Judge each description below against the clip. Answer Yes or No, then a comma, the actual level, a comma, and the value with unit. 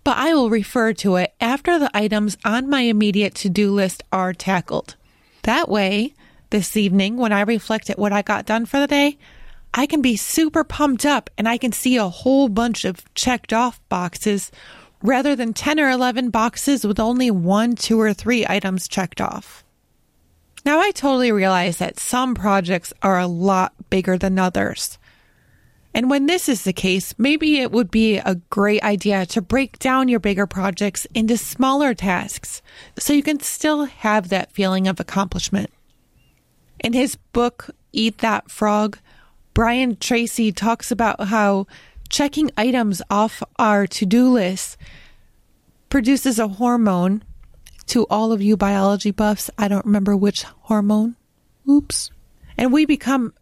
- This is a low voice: No, high, 220 Hz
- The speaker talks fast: No, average, 160 wpm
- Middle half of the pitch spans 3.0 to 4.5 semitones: Yes, average, 4.0 semitones